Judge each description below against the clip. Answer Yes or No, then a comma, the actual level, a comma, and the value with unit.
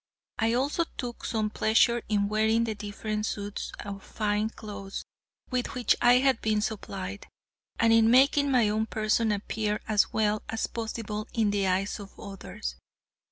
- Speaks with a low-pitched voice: No, high, 215 Hz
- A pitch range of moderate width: No, narrow, 1.8 semitones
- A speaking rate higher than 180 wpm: No, average, 160 wpm